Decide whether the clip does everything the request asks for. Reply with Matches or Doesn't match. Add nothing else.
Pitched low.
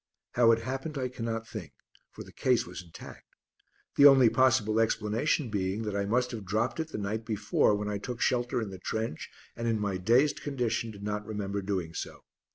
Matches